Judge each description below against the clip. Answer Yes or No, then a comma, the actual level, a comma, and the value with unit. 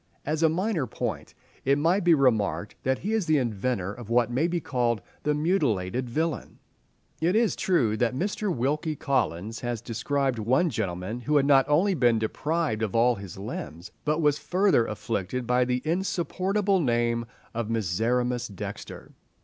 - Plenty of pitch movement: Yes, wide, 5.8 semitones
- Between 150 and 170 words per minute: Yes, average, 165 wpm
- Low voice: Yes, low, 125 Hz